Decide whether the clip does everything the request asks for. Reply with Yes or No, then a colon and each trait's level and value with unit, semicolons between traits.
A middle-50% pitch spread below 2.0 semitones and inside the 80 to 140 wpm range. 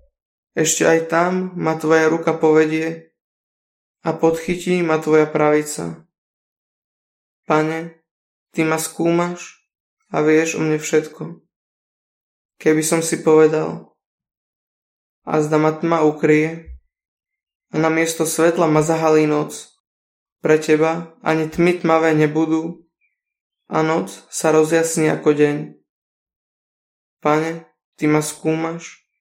Yes: narrow, 1.1 semitones; slow, 110 wpm